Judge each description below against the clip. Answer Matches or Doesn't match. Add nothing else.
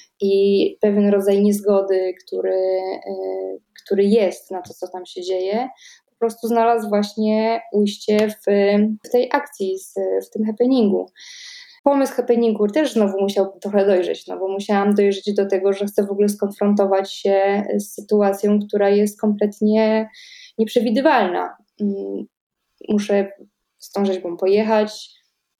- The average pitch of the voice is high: Matches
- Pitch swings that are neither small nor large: Doesn't match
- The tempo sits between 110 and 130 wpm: Matches